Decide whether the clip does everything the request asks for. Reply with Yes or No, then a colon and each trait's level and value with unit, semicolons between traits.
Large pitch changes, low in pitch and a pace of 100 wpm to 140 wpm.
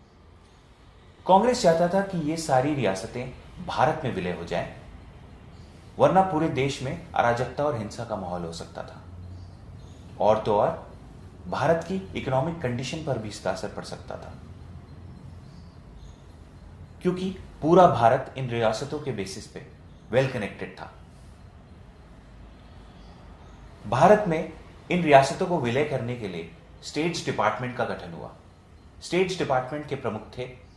Yes: wide, 8.5 semitones; low, 125 Hz; average, 135 wpm